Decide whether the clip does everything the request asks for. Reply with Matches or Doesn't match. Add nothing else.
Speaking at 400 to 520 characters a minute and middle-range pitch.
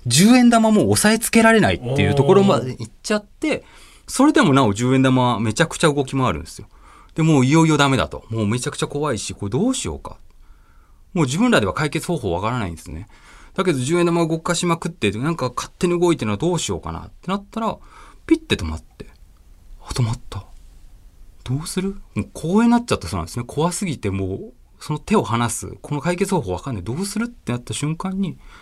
Matches